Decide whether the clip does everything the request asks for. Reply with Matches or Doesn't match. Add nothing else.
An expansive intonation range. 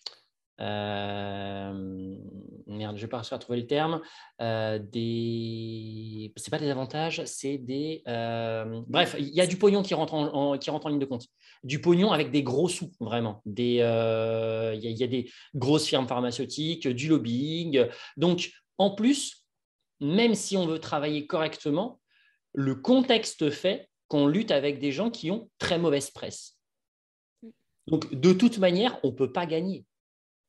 Matches